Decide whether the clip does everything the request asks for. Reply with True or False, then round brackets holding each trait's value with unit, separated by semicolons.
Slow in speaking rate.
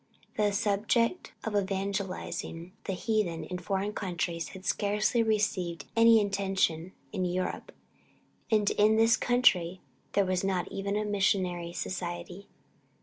True (125 wpm)